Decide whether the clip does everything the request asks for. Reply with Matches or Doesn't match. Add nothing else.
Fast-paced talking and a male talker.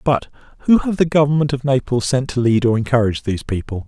Matches